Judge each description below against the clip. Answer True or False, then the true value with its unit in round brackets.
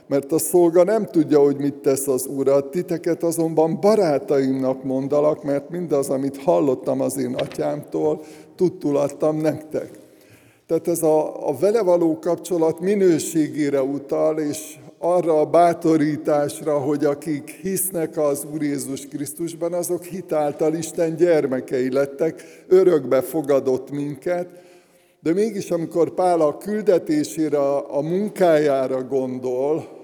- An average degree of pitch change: True (3.4 semitones)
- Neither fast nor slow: True (120 wpm)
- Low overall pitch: False (155 Hz)